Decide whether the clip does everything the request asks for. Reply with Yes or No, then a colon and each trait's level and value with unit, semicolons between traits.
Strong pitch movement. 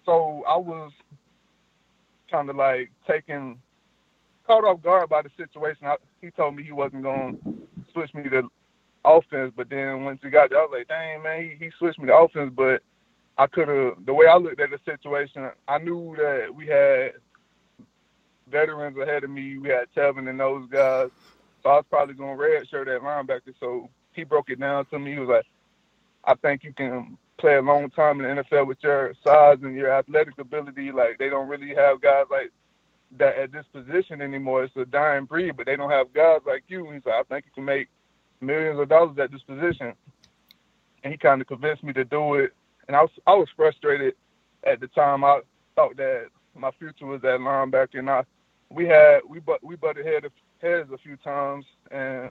No: average, 3.2 semitones